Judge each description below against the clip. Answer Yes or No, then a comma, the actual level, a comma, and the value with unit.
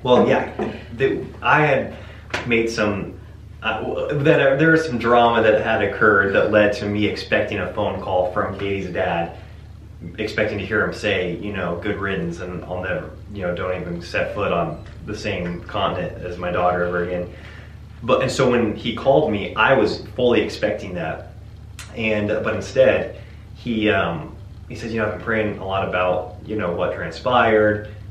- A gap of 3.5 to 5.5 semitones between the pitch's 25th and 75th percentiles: No, average, 3.1 semitones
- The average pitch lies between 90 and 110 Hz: Yes, low, 100 Hz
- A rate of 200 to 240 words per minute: No, average, 175 wpm